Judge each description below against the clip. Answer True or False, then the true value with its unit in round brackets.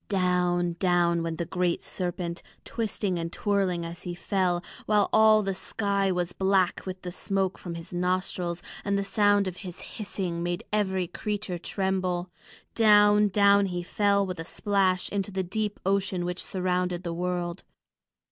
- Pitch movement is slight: True (2.2 semitones)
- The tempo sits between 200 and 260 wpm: False (165 wpm)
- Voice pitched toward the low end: False (185 Hz)